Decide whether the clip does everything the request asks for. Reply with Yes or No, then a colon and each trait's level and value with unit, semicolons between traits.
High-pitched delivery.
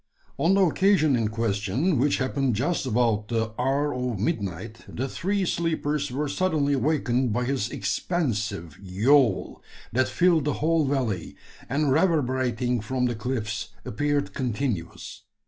No: low, 130 Hz